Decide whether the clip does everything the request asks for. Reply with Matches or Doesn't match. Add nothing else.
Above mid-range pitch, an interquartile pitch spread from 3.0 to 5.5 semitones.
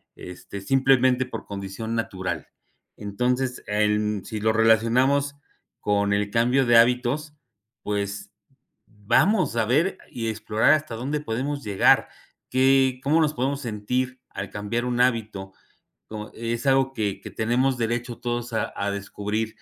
Doesn't match